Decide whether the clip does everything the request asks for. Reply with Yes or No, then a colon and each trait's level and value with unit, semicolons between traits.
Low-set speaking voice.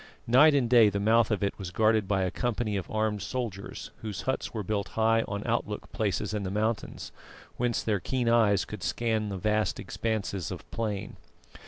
Yes: low, 110 Hz